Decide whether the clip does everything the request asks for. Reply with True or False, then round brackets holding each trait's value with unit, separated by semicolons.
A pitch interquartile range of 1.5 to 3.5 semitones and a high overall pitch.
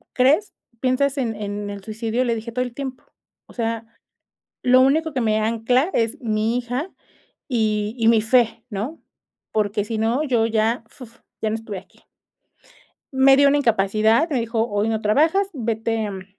True (2.8 semitones; 230 Hz)